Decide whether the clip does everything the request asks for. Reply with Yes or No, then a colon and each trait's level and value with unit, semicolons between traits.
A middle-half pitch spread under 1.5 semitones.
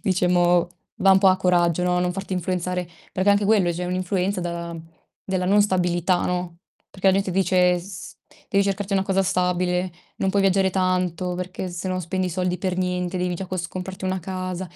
Yes: narrow, 1.1 semitones